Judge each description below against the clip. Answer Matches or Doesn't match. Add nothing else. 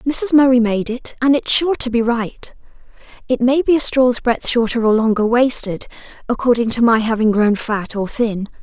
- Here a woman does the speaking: Matches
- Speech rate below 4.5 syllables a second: Doesn't match